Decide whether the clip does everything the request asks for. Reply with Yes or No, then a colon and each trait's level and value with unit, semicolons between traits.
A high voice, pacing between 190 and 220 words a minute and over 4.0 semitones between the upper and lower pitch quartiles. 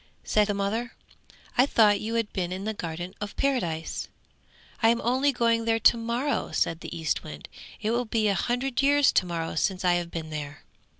Yes: high, 215 Hz; average, 195 wpm; average, 5.2 semitones